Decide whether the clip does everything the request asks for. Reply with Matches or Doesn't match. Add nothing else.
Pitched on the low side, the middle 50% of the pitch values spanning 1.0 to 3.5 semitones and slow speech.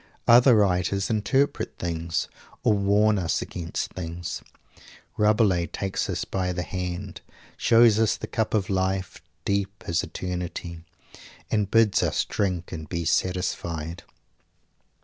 Matches